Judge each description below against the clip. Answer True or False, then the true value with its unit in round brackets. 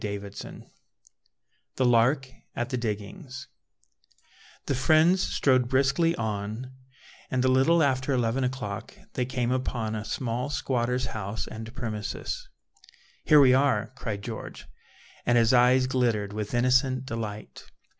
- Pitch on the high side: False (125 Hz)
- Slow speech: True (125 wpm)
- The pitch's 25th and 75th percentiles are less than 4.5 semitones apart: True (2.9 semitones)